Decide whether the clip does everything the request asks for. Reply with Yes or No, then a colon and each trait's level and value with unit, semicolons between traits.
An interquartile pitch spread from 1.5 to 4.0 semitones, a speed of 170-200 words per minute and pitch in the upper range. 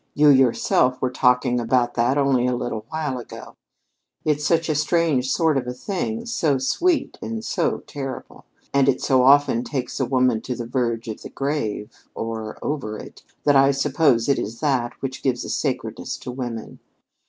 No: average, 3.2 semitones; average, 180 wpm; low, 130 Hz